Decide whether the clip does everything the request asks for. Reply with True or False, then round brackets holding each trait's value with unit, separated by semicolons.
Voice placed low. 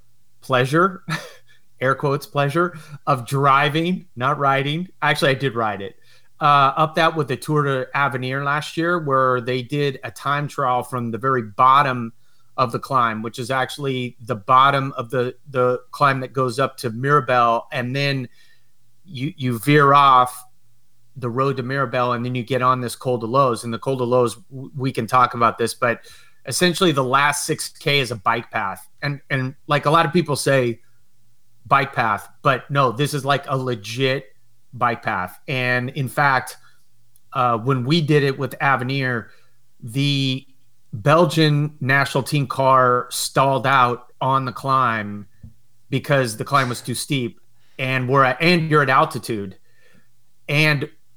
True (130 Hz)